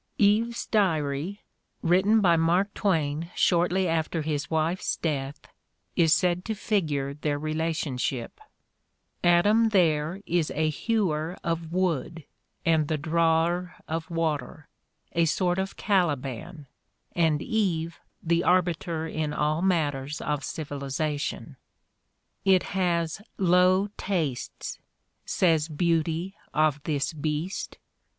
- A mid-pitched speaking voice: Yes, medium, 165 Hz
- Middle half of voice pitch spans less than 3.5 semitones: Yes, average, 3.0 semitones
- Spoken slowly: Yes, slow, 110 wpm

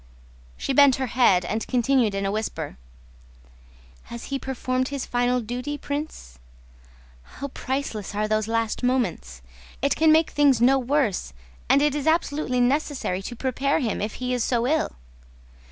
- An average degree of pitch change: Yes, average, 4.2 semitones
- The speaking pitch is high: Yes, very high, 250 Hz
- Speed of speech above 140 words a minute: Yes, average, 155 wpm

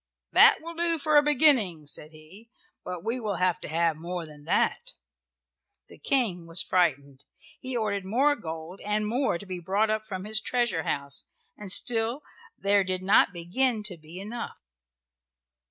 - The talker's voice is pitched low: No, high, 195 Hz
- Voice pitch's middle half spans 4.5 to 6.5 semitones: Yes, wide, 5.5 semitones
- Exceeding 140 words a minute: Yes, average, 170 wpm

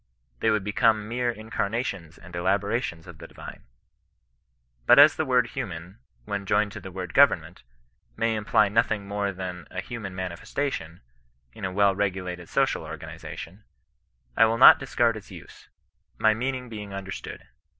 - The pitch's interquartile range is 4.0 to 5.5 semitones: No, average, 3.6 semitones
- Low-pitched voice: Yes, low, 100 Hz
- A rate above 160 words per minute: No, average, 155 wpm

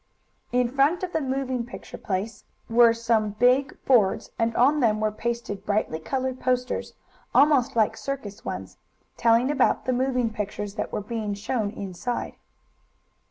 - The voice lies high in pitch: Yes, high, 235 Hz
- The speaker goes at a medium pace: Yes, average, 150 wpm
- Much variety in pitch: No, average, 3.4 semitones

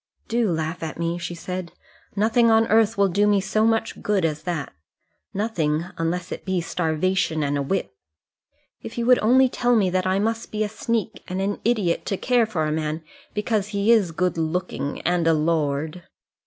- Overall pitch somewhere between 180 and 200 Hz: Yes, medium, 185 Hz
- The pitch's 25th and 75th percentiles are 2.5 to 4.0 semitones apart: No, average, 4.9 semitones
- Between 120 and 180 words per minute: No, average, 195 wpm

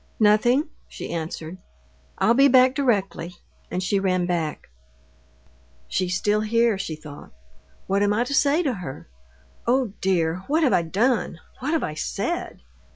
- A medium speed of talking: Yes, average, 155 wpm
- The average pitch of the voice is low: No, high, 205 Hz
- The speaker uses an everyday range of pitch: No, wide, 6.1 semitones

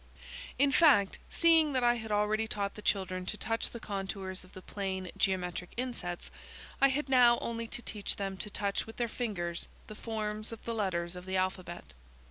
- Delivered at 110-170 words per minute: No, average, 190 wpm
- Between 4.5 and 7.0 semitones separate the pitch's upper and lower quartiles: No, average, 3.8 semitones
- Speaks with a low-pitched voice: No, high, 210 Hz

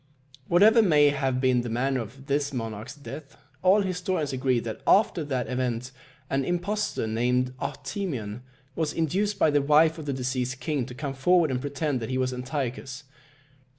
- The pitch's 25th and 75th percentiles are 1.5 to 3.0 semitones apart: No, average, 4.1 semitones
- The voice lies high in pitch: No, low, 135 Hz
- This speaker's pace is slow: No, average, 170 wpm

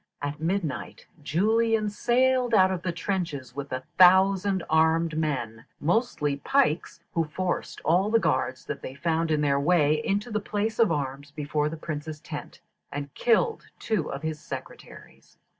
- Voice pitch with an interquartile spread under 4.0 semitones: No, wide, 5.5 semitones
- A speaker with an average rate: Yes, average, 160 wpm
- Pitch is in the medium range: Yes, medium, 165 Hz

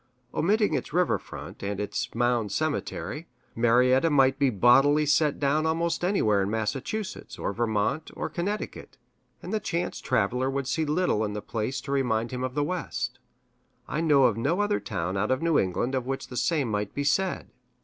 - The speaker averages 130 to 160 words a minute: No, average, 185 wpm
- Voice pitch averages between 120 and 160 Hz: Yes, low, 135 Hz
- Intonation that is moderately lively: No, wide, 6.0 semitones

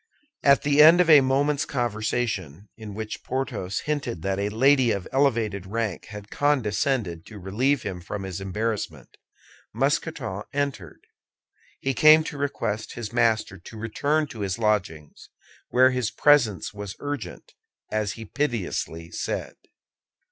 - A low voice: Yes, low, 115 Hz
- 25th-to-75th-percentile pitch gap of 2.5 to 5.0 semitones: No, wide, 5.6 semitones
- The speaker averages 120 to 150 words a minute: Yes, average, 140 wpm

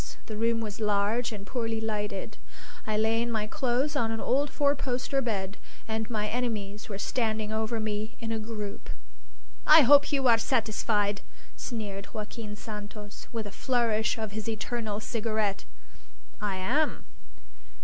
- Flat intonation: Yes, narrow, 2.1 semitones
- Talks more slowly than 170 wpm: Yes, average, 150 wpm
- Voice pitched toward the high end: Yes, high, 220 Hz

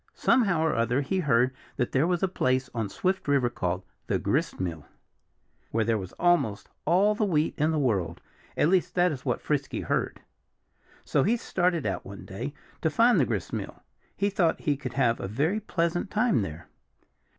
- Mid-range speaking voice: Yes, medium, 145 Hz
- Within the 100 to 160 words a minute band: No, average, 185 wpm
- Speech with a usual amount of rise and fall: No, wide, 7.7 semitones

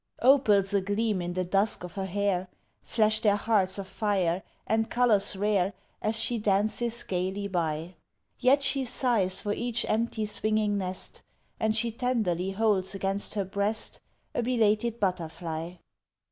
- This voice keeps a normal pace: Yes, average, 145 wpm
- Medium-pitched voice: No, high, 205 Hz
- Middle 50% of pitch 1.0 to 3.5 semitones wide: Yes, average, 2.9 semitones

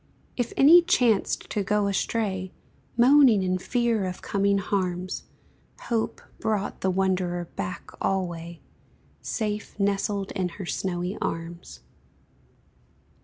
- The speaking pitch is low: No, high, 195 Hz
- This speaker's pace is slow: Yes, slow, 110 wpm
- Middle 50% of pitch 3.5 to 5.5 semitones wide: No, average, 2.8 semitones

